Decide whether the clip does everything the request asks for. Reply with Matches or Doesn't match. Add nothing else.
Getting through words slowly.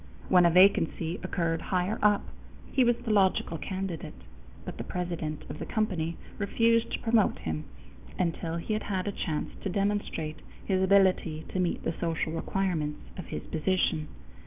Doesn't match